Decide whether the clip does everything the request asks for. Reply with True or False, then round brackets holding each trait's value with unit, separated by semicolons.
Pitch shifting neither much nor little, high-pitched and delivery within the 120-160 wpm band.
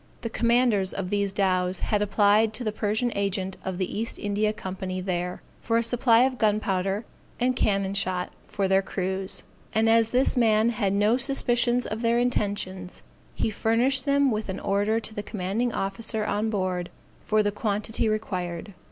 False (3.0 semitones; 210 Hz; 170 wpm)